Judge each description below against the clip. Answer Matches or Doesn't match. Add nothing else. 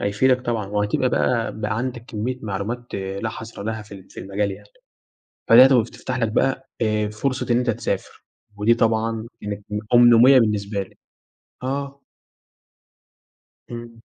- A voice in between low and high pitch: Doesn't match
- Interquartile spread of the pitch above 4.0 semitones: Doesn't match